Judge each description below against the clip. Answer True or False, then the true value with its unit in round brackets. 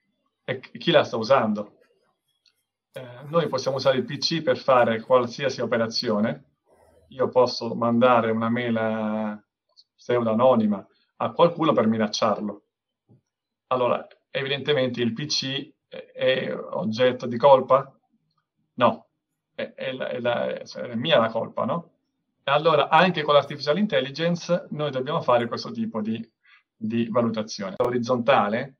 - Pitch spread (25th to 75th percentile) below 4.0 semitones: False (4.4 semitones)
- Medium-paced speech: True (125 wpm)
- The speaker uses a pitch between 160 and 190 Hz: False (125 Hz)